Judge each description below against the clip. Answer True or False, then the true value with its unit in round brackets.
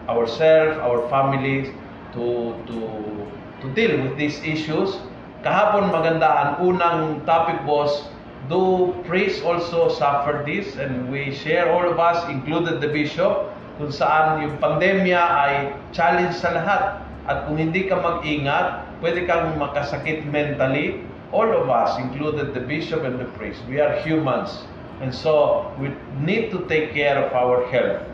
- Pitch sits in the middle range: True (150 Hz)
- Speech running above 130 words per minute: True (145 wpm)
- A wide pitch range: False (3.7 semitones)